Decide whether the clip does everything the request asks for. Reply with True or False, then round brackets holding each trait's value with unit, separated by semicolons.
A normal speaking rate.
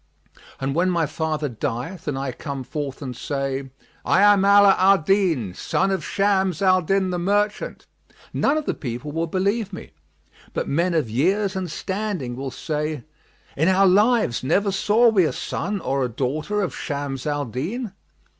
True (175 wpm)